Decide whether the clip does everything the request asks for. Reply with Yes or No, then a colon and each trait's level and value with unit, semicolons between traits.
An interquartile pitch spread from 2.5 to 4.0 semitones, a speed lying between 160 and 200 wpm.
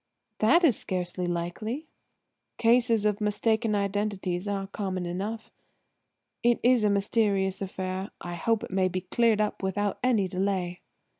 No: average, 2.9 semitones; slow, 135 wpm